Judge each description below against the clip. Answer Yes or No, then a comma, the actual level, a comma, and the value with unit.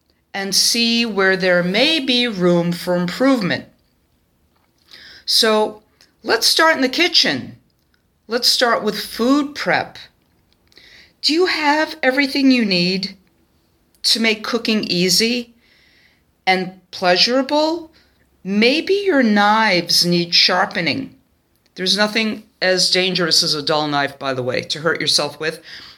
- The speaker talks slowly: Yes, slow, 120 wpm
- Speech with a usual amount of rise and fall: No, wide, 6.2 semitones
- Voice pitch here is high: Yes, high, 210 Hz